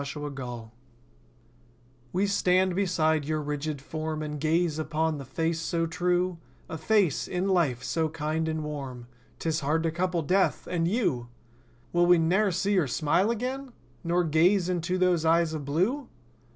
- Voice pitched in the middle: Yes, medium, 165 Hz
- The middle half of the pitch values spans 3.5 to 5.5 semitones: No, average, 3.1 semitones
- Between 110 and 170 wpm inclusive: Yes, average, 150 wpm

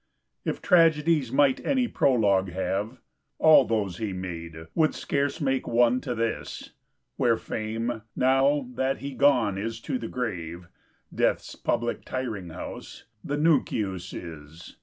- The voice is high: No, low, 115 Hz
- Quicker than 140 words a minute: No, slow, 135 wpm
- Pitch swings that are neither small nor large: No, wide, 6.3 semitones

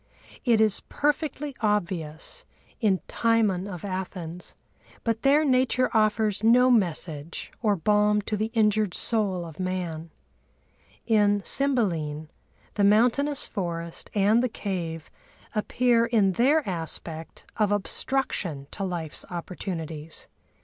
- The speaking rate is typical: No, slow, 110 wpm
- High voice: Yes, high, 205 Hz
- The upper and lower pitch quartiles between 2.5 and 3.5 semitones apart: No, average, 4.9 semitones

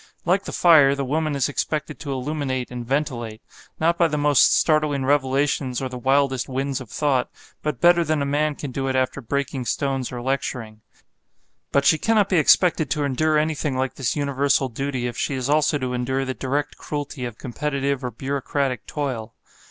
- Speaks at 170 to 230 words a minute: Yes, average, 190 wpm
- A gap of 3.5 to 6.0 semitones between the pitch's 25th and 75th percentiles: No, narrow, 2.4 semitones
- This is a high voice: No, medium, 140 Hz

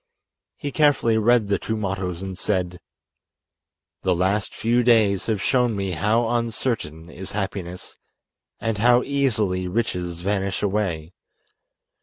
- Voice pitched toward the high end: No, low, 100 Hz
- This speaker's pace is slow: Yes, slow, 125 wpm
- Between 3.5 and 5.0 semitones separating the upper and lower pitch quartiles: Yes, average, 4.0 semitones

